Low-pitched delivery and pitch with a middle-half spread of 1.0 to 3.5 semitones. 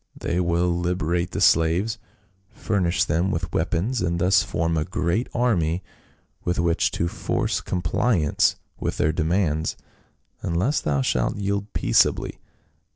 Yes: very low, 85 Hz; narrow, 2.5 semitones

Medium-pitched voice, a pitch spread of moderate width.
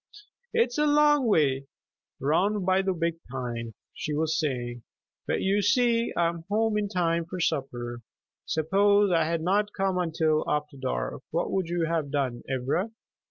No: medium, 170 Hz; wide, 6.0 semitones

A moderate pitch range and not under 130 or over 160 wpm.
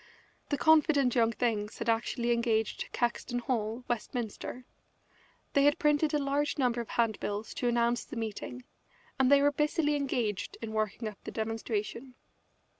Yes: average, 3.8 semitones; average, 155 wpm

